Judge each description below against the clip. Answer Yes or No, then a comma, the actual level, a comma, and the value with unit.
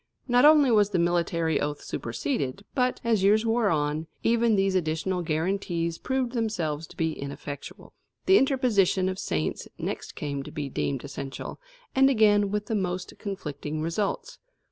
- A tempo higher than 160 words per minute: No, average, 155 wpm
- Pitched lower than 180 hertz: No, medium, 185 Hz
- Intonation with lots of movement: Yes, wide, 6.2 semitones